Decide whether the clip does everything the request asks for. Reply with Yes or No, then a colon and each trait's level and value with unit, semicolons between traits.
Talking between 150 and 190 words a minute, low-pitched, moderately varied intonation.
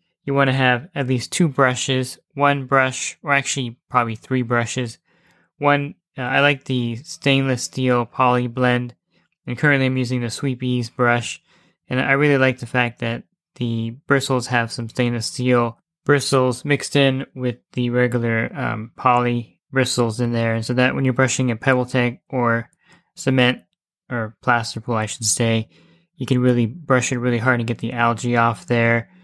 No: average, 175 wpm; low, 125 Hz; narrow, 2.2 semitones